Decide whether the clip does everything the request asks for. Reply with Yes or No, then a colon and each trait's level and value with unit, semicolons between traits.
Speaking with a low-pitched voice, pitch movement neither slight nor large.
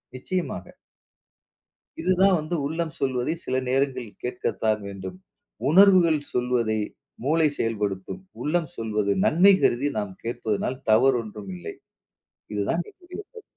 No: low, 130 Hz; wide, 7.3 semitones